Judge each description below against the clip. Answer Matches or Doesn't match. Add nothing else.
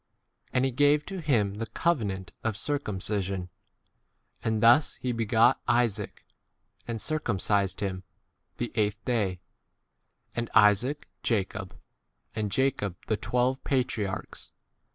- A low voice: Matches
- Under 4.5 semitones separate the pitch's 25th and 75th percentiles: Matches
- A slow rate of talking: Matches